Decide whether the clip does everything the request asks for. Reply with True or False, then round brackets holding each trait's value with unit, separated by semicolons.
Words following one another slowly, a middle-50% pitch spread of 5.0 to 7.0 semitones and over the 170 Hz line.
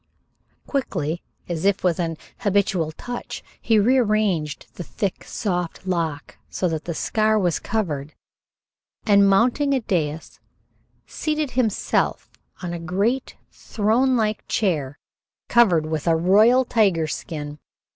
True (120 wpm; 5.3 semitones; 190 Hz)